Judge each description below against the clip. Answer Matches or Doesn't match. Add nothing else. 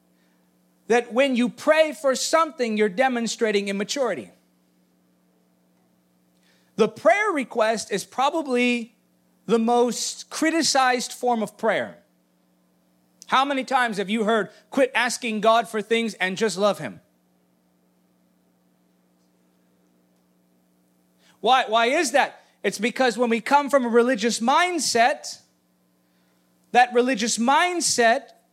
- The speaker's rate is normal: Doesn't match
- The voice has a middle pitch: Doesn't match